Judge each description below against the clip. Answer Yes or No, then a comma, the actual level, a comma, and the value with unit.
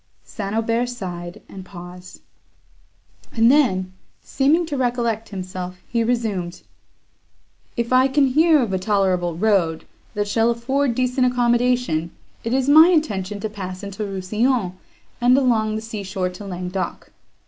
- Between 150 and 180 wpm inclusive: No, average, 140 wpm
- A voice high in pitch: Yes, high, 220 Hz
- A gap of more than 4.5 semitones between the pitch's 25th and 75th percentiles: Yes, average, 4.9 semitones